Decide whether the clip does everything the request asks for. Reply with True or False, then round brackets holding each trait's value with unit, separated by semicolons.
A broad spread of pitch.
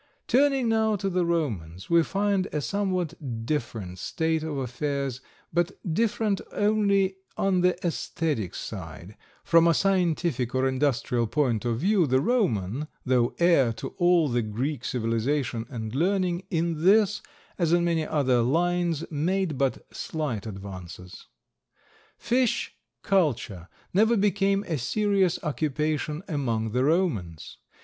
True (7.4 semitones)